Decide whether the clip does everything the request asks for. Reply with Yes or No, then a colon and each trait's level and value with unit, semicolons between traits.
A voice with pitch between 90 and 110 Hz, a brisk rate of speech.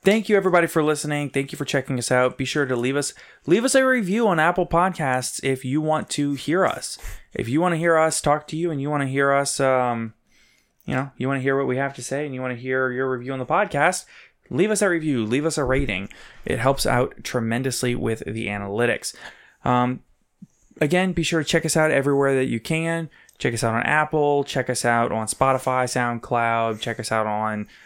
No: low, 135 Hz; fast, 235 wpm